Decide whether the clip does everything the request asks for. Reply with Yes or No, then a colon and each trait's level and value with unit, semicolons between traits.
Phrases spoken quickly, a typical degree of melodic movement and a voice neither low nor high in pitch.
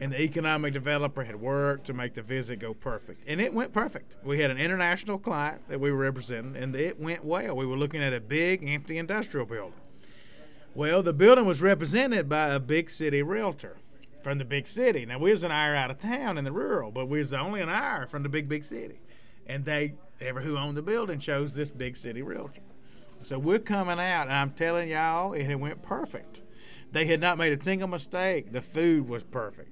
Yes: fast, 220 wpm; average, 4.3 semitones; medium, 150 Hz